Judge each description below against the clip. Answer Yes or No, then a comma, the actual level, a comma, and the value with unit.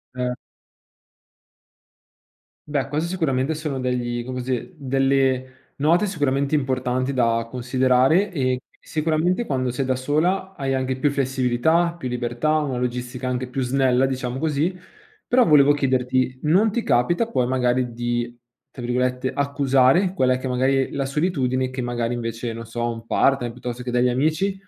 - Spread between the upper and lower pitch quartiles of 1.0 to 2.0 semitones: No, average, 2.7 semitones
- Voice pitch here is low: Yes, low, 130 Hz